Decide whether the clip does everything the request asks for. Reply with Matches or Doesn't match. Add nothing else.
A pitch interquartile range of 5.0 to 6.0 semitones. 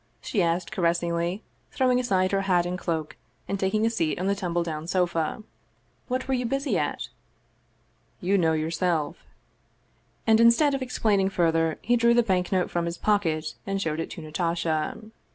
Doesn't match